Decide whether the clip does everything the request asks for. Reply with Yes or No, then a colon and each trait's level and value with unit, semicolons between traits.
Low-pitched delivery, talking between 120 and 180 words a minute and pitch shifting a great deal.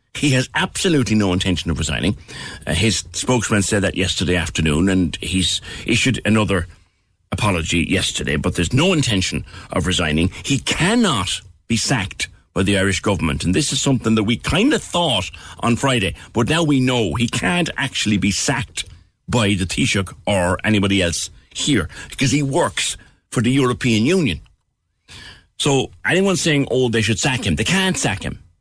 Yes: low, 100 Hz; average, 170 wpm; wide, 6.1 semitones